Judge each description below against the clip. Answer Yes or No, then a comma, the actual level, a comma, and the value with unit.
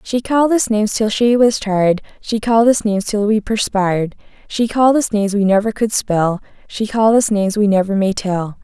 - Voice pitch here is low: No, high, 210 Hz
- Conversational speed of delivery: No, fast, 215 wpm